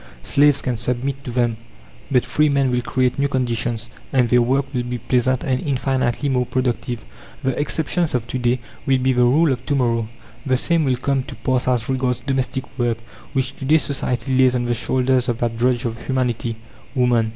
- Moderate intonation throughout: No, narrow, 1.7 semitones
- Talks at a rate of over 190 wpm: Yes, average, 200 wpm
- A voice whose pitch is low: Yes, low, 125 Hz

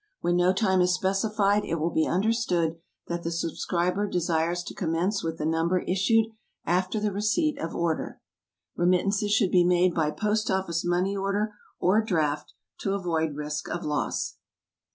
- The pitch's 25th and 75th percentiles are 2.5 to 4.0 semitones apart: Yes, average, 3.1 semitones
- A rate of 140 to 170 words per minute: Yes, average, 160 wpm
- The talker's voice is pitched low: No, medium, 180 Hz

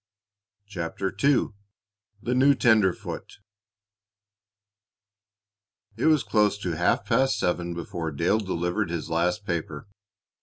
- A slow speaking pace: Yes, slow, 105 wpm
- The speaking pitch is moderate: No, very low, 95 Hz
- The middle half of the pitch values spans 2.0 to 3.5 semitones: No, average, 4.2 semitones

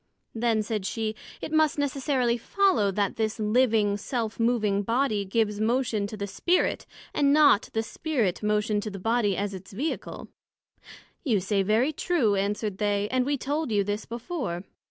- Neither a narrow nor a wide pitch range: Yes, average, 4.0 semitones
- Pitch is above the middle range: Yes, high, 220 Hz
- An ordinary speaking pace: Yes, average, 165 wpm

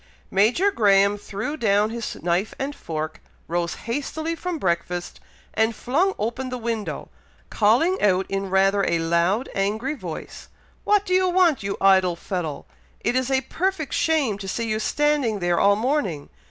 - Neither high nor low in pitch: No, high, 215 Hz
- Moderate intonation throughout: No, wide, 6.9 semitones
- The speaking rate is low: No, average, 160 wpm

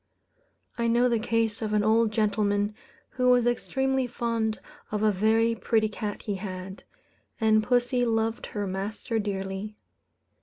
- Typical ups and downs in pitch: No, narrow, 2.1 semitones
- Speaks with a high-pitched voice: Yes, high, 220 Hz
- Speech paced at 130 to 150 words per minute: Yes, average, 145 wpm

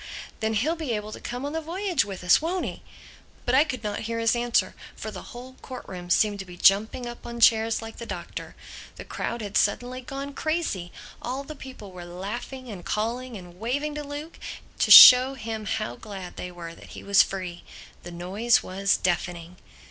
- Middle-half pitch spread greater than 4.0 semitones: Yes, average, 5.1 semitones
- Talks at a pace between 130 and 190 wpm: No, average, 200 wpm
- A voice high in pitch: Yes, high, 225 Hz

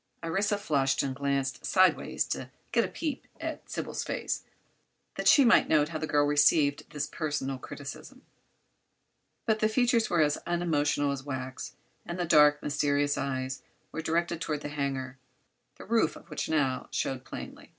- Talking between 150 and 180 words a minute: Yes, average, 160 wpm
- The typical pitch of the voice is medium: Yes, medium, 150 Hz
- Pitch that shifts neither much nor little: Yes, average, 3.6 semitones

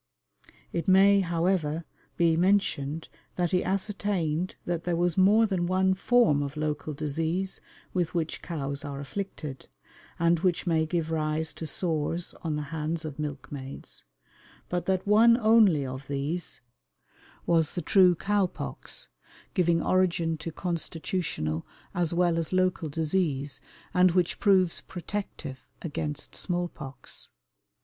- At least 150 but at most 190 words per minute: No, slow, 135 wpm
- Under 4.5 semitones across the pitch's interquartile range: Yes, average, 3.3 semitones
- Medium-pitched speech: Yes, medium, 170 Hz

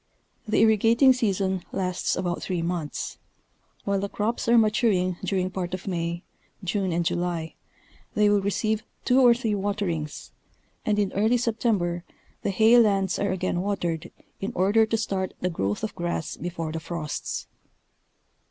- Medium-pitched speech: No, high, 195 Hz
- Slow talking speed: No, average, 150 wpm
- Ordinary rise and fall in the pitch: Yes, average, 3.6 semitones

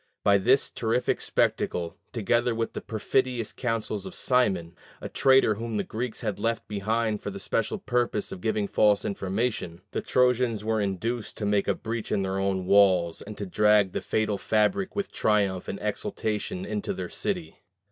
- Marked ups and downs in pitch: No, average, 3.3 semitones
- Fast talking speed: No, average, 175 wpm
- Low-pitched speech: Yes, low, 110 Hz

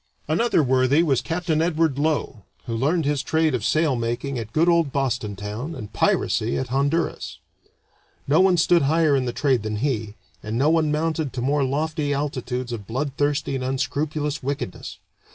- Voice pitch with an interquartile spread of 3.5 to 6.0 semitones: Yes, average, 3.9 semitones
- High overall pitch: No, medium, 140 Hz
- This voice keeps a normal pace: Yes, average, 170 wpm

